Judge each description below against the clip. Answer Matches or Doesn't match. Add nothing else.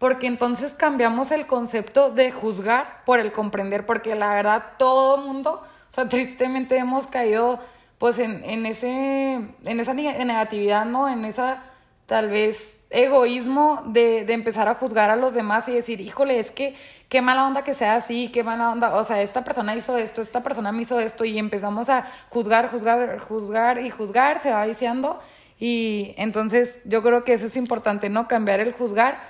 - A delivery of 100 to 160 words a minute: Doesn't match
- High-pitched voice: Matches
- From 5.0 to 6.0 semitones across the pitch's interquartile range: Doesn't match